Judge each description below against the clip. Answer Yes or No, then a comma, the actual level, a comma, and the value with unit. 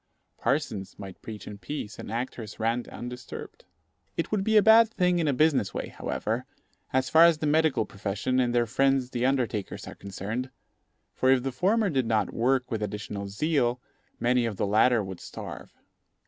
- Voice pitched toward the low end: Yes, low, 125 Hz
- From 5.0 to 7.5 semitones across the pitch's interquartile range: Yes, average, 5.3 semitones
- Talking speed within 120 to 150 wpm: No, average, 180 wpm